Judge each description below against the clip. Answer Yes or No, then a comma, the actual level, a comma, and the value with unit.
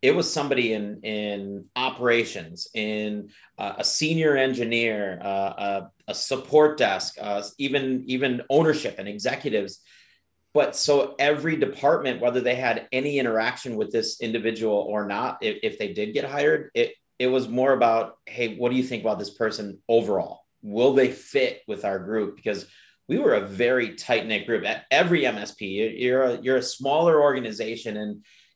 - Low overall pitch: Yes, low, 120 Hz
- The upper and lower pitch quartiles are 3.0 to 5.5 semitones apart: Yes, average, 4.3 semitones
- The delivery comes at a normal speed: Yes, average, 170 wpm